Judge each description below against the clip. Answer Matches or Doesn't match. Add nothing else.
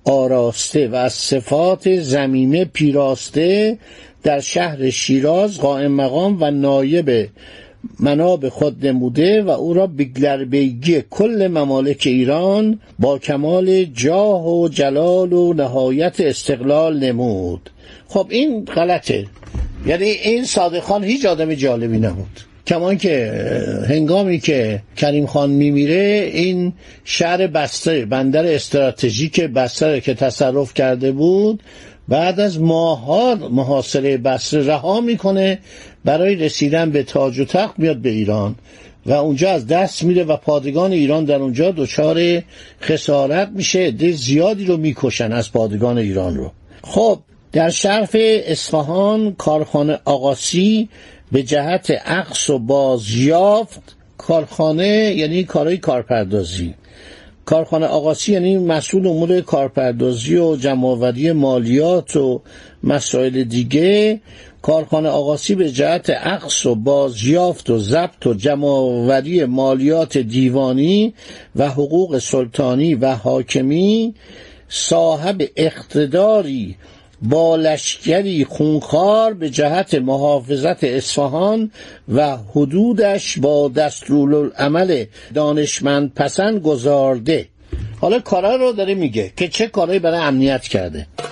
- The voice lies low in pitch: Doesn't match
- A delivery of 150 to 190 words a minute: Doesn't match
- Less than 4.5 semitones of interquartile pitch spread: Doesn't match